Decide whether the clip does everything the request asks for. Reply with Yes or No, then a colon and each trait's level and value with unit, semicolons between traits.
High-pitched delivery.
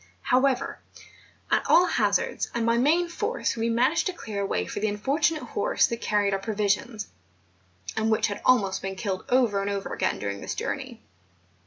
Yes: high, 225 Hz